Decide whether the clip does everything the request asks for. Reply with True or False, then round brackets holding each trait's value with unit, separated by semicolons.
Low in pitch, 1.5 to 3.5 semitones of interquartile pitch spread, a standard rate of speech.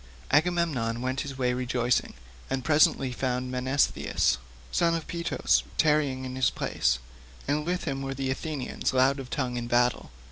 True (130 Hz; 2.8 semitones; 155 wpm)